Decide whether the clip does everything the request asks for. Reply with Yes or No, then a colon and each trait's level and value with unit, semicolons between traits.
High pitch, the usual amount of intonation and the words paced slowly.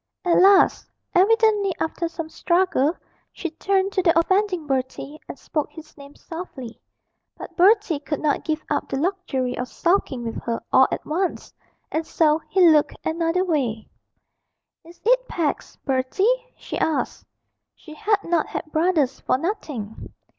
No: very high, 330 Hz; average, 4.7 semitones; average, 150 wpm